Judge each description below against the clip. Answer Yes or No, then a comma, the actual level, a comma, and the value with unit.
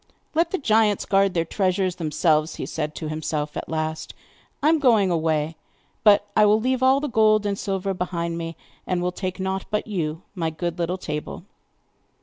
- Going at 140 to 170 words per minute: No, average, 185 wpm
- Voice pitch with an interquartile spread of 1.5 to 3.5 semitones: No, average, 4.4 semitones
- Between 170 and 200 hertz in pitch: Yes, medium, 185 Hz